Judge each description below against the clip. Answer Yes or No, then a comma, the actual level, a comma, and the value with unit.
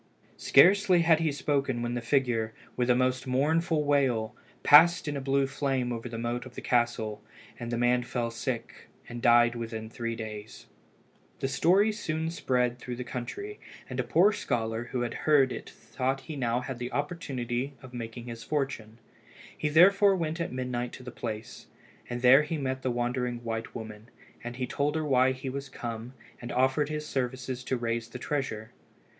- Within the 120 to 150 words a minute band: No, average, 185 wpm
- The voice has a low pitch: Yes, low, 125 Hz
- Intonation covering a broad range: No, average, 3.2 semitones